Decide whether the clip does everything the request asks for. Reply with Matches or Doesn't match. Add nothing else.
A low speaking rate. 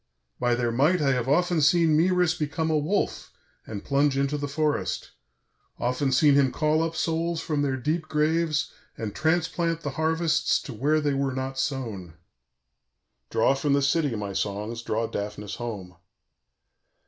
Doesn't match